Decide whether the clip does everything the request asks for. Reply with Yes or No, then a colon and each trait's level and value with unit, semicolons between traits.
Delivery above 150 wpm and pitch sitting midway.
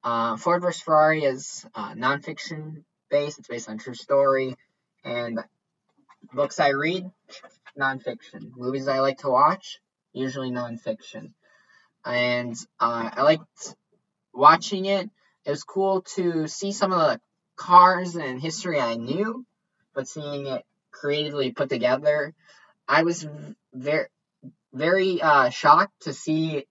No: slow, 135 wpm; medium, 150 Hz